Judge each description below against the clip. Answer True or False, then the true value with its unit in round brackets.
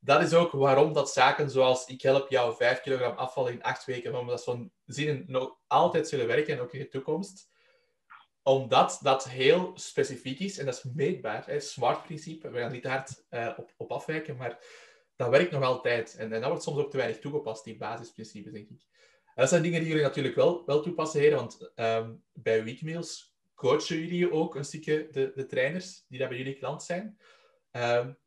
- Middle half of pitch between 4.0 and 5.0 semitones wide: True (4.7 semitones)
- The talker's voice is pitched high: False (145 Hz)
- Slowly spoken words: False (200 wpm)